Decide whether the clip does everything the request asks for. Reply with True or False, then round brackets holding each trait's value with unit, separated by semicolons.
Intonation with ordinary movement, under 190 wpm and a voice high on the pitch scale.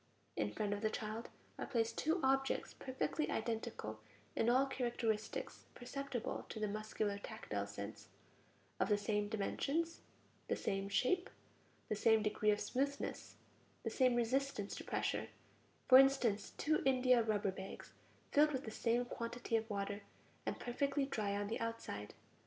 True (4.1 semitones; 150 wpm; 225 Hz)